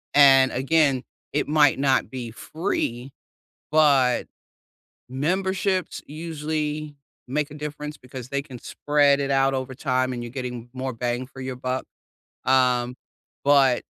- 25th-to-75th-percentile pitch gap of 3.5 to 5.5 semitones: No, average, 2.7 semitones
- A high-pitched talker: No, low, 135 Hz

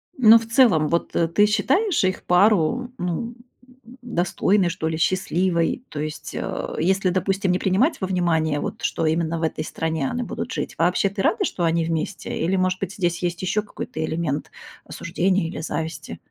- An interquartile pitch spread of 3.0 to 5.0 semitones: Yes, average, 4.0 semitones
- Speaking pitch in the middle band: Yes, medium, 180 Hz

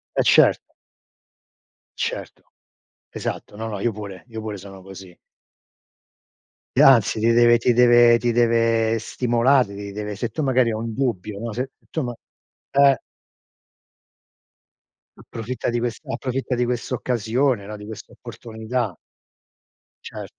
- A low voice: Yes, low, 115 Hz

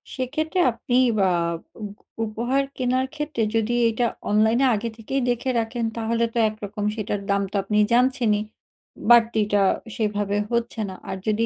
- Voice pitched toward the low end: No, high, 230 Hz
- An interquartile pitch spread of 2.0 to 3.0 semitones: Yes, average, 2.7 semitones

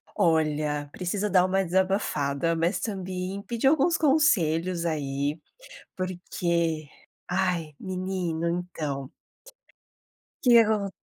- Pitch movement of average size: Yes, average, 3.5 semitones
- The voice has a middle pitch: Yes, medium, 180 Hz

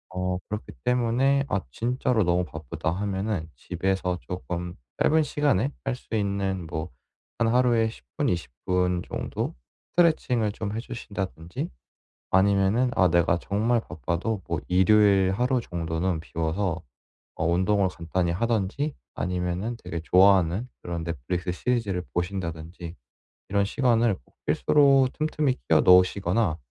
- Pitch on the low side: Yes, very low, 95 Hz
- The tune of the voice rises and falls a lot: No, average, 4.7 semitones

